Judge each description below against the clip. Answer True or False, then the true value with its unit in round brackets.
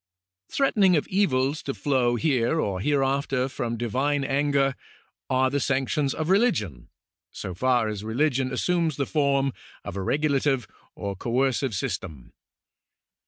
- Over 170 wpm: False (135 wpm)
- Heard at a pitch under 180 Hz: True (135 Hz)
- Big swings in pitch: False (3.3 semitones)